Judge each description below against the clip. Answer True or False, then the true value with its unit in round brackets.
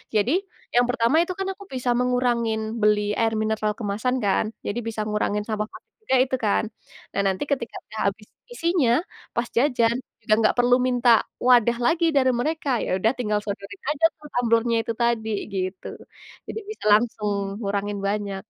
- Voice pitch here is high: True (230 Hz)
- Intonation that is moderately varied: True (3.0 semitones)